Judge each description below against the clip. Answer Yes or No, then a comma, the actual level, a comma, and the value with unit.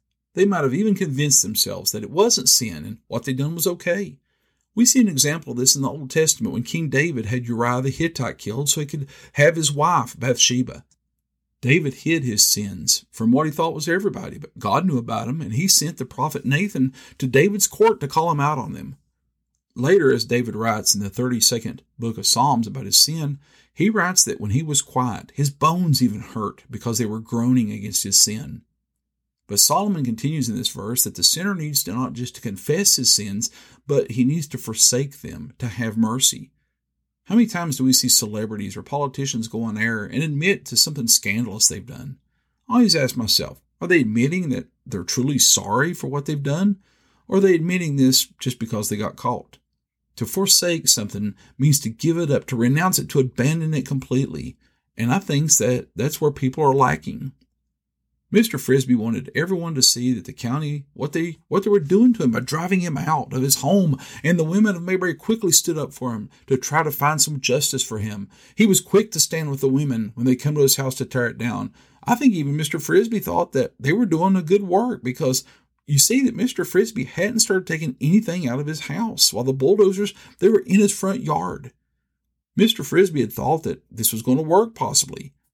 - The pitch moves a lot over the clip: Yes, wide, 6.0 semitones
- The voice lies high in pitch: No, low, 135 Hz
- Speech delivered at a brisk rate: Yes, fast, 215 wpm